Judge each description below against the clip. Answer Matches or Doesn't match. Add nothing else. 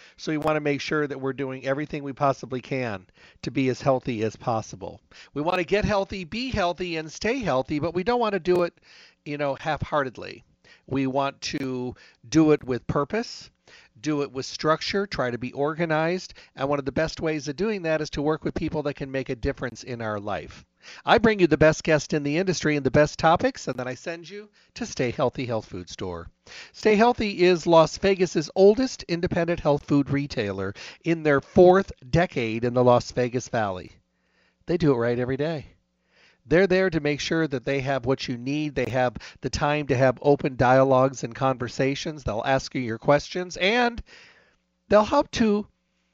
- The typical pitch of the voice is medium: Matches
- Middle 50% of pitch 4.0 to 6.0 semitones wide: Matches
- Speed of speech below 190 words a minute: Doesn't match